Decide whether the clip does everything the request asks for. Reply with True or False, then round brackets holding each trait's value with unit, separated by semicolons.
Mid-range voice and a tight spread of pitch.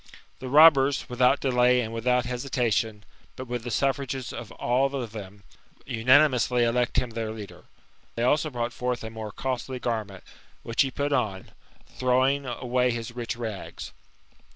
False (125 Hz; 2.2 semitones)